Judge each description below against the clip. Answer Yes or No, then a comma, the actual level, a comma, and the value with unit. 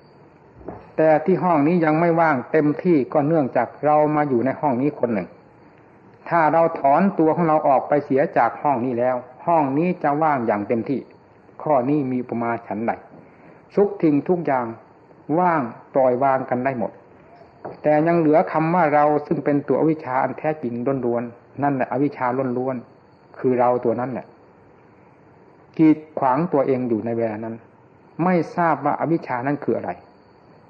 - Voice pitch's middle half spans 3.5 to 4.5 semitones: Yes, average, 4.0 semitones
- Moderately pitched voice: Yes, medium, 145 Hz